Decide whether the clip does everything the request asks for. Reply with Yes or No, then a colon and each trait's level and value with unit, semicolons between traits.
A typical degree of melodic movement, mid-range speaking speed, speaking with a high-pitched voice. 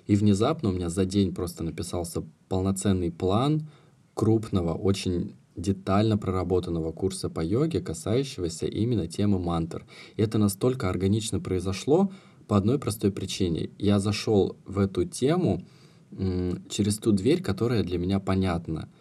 No: average, 3.0 semitones; average, 135 wpm; low, 100 Hz